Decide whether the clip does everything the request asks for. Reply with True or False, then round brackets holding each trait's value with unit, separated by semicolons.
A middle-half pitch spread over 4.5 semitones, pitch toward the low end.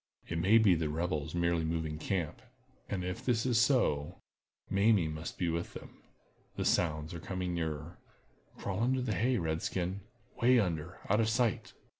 True (5.4 semitones; 90 Hz)